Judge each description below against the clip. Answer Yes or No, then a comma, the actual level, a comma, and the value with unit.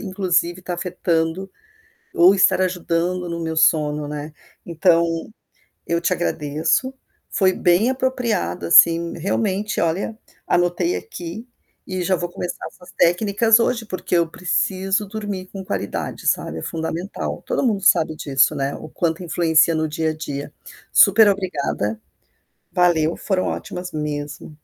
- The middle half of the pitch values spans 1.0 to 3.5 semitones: Yes, average, 3.0 semitones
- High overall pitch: No, medium, 175 Hz